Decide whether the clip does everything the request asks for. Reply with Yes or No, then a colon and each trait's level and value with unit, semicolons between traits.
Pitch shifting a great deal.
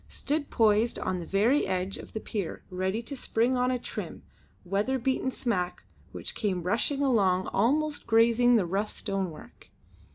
No: average, 4.8 semitones